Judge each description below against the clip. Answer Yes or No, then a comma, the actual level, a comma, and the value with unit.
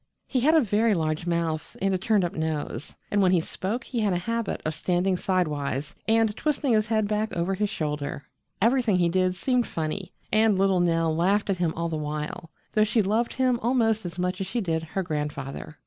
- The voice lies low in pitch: No, medium, 185 Hz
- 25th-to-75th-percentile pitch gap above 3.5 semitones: Yes, average, 4.9 semitones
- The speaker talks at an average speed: No, fast, 210 wpm